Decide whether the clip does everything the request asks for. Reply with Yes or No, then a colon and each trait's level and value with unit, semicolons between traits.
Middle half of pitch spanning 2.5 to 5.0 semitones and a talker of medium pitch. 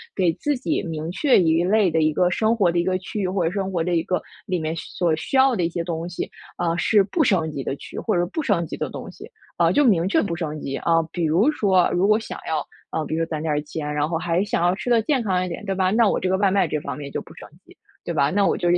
Yes: average, 3.7 semitones; medium, 180 Hz